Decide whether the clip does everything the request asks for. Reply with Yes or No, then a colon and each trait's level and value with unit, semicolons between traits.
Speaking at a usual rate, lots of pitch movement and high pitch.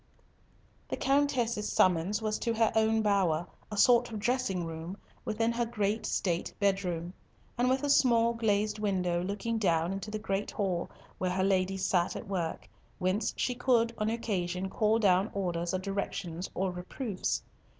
No: average, 165 wpm; average, 3.7 semitones; high, 200 Hz